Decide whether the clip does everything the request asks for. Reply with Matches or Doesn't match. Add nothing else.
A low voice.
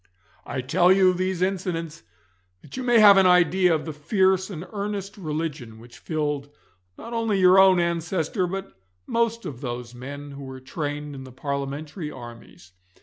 Doesn't match